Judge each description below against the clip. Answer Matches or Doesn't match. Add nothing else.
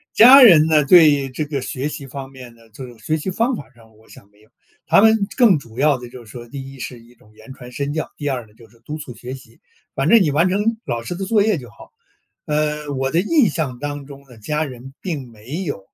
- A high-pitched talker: Doesn't match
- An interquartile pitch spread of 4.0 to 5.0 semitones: Matches